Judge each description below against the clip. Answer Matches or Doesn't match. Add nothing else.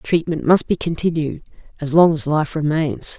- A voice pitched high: Doesn't match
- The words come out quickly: Doesn't match